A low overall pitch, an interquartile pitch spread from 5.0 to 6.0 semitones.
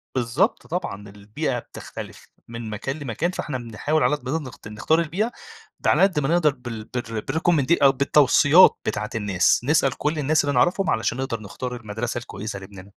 Yes: low, 130 Hz; wide, 5.4 semitones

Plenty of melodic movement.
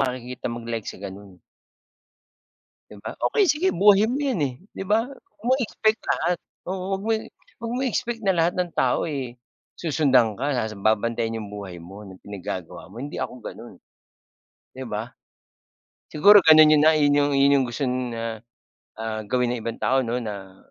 Yes: wide, 8.0 semitones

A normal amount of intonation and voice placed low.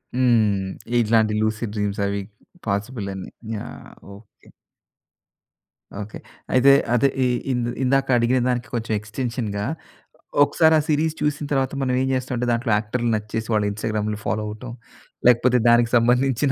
Yes: average, 3.1 semitones; low, 120 Hz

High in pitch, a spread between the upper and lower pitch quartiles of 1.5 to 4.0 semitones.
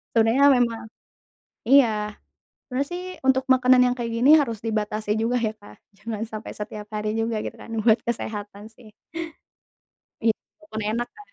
Yes: high, 230 Hz; average, 2.8 semitones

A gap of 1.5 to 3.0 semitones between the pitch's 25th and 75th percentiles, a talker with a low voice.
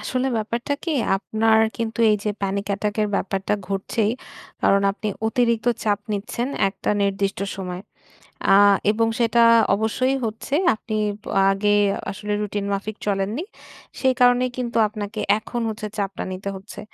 No: average, 2.7 semitones; high, 210 Hz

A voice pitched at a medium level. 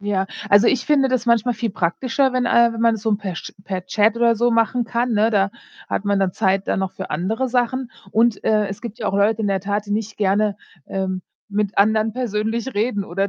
No: high, 215 Hz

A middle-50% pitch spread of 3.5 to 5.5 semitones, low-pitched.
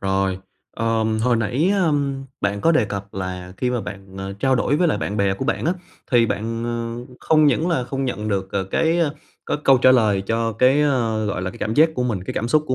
Yes: average, 5.0 semitones; low, 115 Hz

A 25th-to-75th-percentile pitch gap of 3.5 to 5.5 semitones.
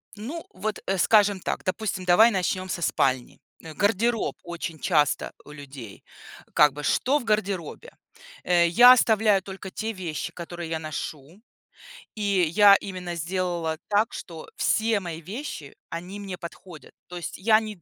Yes: average, 4.0 semitones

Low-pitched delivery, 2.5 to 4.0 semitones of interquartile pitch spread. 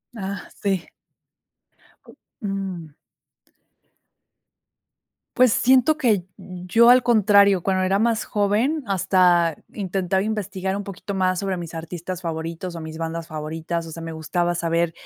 No: medium, 185 Hz; average, 3.3 semitones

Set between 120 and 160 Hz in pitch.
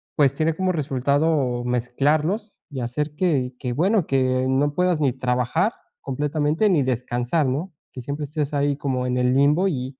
Yes: medium, 140 Hz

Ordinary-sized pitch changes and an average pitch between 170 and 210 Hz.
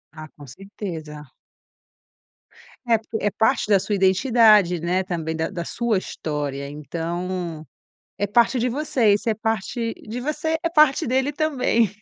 No: wide, 5.8 semitones; high, 205 Hz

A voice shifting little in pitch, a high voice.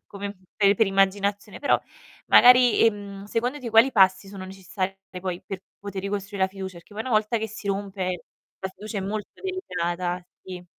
Yes: narrow, 2.2 semitones; high, 200 Hz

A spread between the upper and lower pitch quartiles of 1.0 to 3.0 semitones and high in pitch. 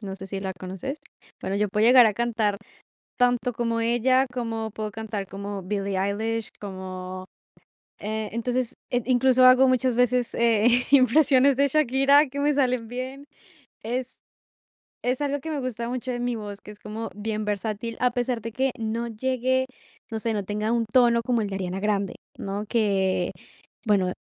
No: average, 3.5 semitones; high, 230 Hz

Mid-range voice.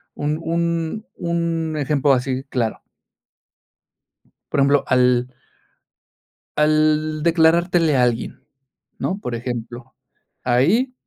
Yes: medium, 150 Hz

